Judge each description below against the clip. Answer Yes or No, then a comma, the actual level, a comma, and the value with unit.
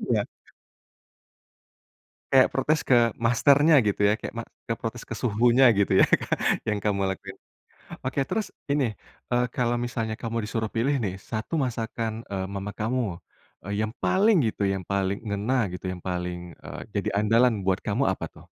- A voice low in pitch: Yes, low, 115 Hz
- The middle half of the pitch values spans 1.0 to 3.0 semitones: No, average, 3.7 semitones